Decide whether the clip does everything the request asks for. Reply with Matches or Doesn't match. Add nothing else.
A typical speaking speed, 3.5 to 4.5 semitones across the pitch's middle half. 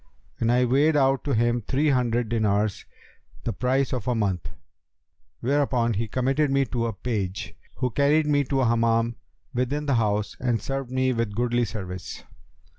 Doesn't match